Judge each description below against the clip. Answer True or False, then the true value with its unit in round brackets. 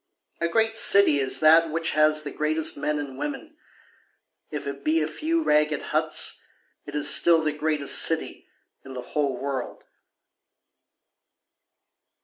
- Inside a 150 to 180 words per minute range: False (140 wpm)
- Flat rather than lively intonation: True (2.3 semitones)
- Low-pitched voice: False (155 Hz)